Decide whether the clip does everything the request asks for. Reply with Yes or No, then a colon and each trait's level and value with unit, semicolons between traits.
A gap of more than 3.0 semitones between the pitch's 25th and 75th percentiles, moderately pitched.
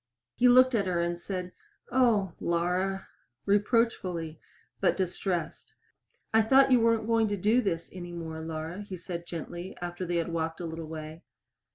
Yes: average, 4.1 semitones; medium, 180 Hz